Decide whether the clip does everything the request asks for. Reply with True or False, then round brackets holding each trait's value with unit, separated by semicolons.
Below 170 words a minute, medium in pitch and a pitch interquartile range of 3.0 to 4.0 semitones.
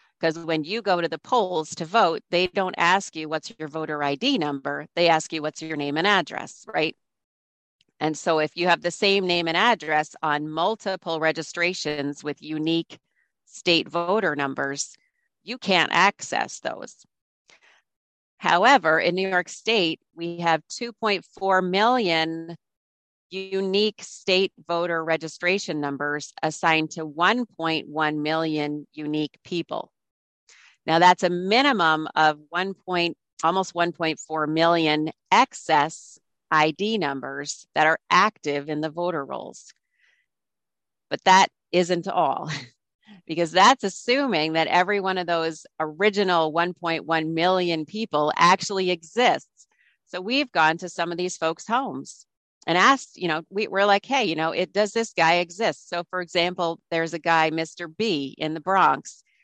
True (145 wpm; 170 Hz; 3.3 semitones)